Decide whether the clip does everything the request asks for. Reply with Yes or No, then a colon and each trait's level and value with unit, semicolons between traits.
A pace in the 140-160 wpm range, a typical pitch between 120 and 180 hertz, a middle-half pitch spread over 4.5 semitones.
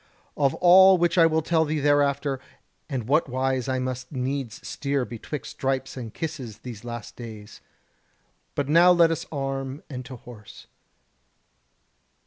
No: average, 145 wpm; low, 135 Hz; average, 3.5 semitones